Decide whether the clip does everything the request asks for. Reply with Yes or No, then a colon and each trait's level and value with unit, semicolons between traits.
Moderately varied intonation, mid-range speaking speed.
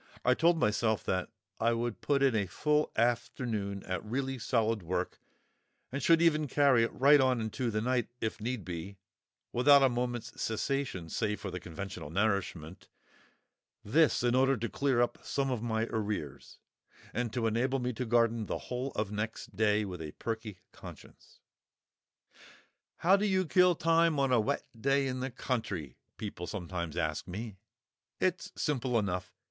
Yes: average, 4.4 semitones; average, 160 wpm